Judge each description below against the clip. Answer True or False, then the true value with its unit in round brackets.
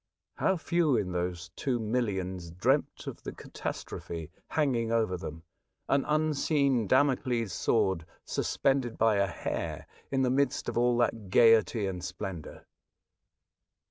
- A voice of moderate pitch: False (115 Hz)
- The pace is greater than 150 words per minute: False (135 wpm)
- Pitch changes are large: True (6.3 semitones)